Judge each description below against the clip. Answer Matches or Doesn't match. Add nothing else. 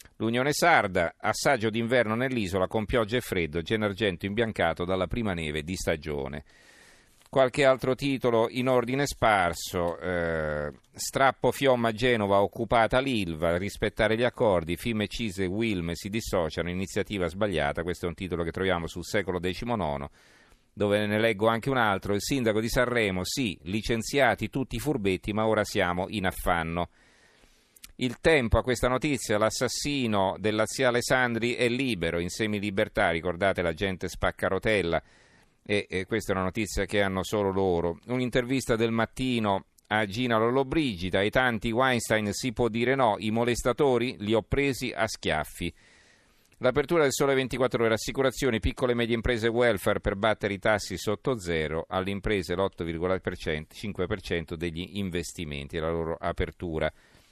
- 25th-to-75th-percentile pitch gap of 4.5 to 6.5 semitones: Matches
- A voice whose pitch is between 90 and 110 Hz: Matches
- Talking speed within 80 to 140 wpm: Doesn't match